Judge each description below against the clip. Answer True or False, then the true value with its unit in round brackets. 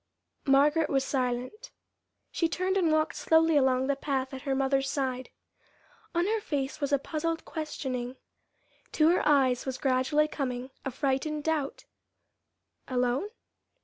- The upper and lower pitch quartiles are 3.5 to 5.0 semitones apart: False (3.1 semitones)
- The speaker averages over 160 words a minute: False (140 wpm)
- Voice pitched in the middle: False (275 Hz)